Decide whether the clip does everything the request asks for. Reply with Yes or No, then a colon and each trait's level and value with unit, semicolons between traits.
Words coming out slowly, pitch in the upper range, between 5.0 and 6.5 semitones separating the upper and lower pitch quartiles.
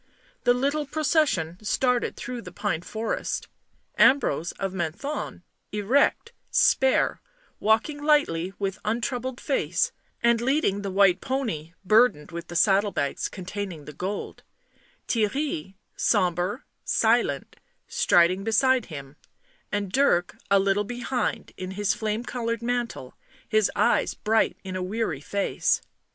Yes: slow, 125 wpm; high, 210 Hz; average, 5.3 semitones